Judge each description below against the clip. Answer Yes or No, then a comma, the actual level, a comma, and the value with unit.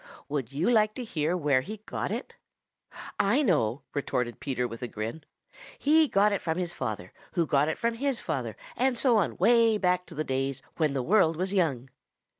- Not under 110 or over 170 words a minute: No, average, 200 wpm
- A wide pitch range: Yes, wide, 7.8 semitones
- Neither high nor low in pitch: Yes, medium, 165 Hz